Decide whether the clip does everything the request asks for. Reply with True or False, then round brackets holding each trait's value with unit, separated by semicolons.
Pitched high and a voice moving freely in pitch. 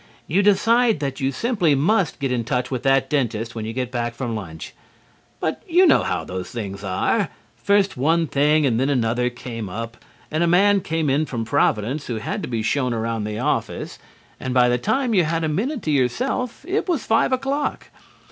False (135 Hz; 8.1 semitones)